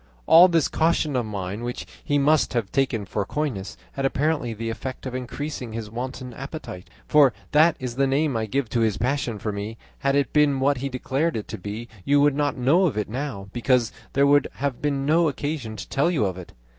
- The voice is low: Yes, low, 130 Hz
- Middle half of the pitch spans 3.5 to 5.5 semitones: Yes, average, 4.2 semitones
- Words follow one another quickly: Yes, fast, 220 wpm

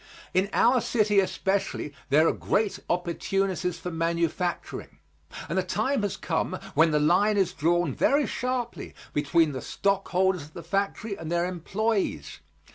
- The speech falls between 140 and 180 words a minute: Yes, average, 145 wpm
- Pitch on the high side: No, medium, 180 Hz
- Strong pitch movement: No, average, 3.4 semitones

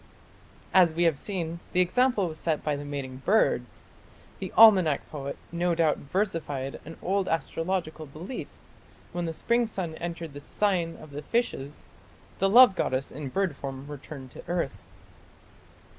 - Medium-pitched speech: Yes, medium, 165 Hz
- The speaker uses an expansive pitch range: No, average, 4.7 semitones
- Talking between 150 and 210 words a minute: Yes, average, 155 wpm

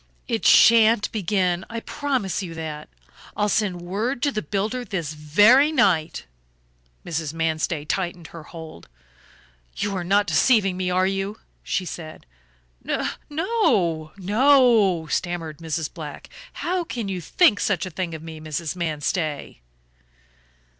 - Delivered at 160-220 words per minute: No, slow, 135 wpm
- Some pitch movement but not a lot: Yes, average, 4.8 semitones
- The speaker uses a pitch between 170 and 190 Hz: Yes, medium, 185 Hz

